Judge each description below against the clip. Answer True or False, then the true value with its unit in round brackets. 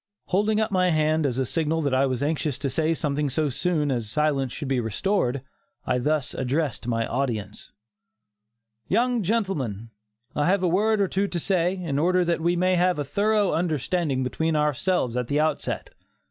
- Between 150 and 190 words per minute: True (185 wpm)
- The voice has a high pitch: False (155 Hz)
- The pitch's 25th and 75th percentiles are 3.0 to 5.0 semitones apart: False (5.4 semitones)